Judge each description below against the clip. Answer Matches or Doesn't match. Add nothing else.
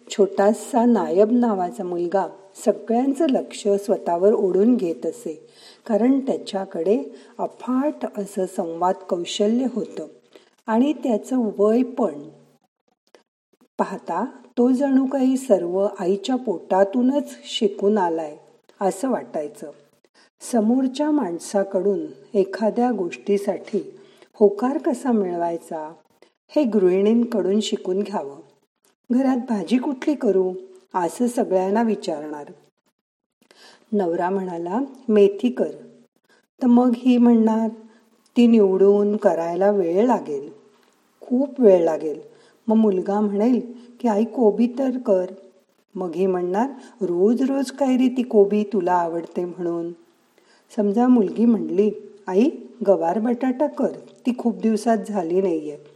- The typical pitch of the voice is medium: Doesn't match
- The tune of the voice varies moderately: Matches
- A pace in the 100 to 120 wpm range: Matches